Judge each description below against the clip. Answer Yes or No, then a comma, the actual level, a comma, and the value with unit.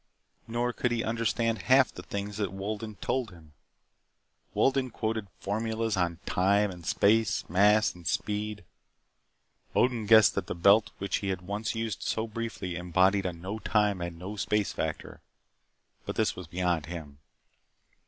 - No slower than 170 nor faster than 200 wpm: No, average, 155 wpm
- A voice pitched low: Yes, low, 105 Hz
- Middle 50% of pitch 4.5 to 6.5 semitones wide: No, average, 3.6 semitones